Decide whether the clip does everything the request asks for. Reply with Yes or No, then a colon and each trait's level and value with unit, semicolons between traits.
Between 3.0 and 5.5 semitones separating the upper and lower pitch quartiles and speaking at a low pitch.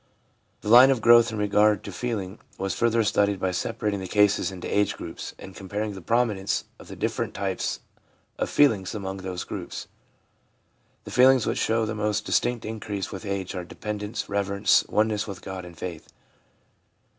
No: narrow, 2.5 semitones; low, 105 Hz